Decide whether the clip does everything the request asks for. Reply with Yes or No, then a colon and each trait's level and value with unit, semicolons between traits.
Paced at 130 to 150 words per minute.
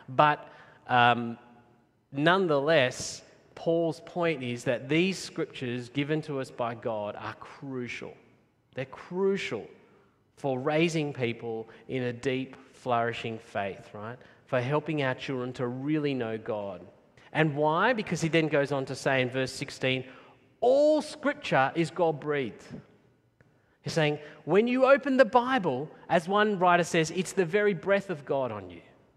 Yes: average, 145 wpm